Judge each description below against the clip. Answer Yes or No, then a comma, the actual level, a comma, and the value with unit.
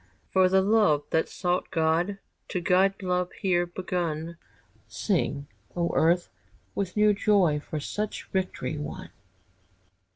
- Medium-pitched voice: Yes, medium, 180 Hz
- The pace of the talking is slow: Yes, slow, 125 wpm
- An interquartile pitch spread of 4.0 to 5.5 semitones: No, average, 2.8 semitones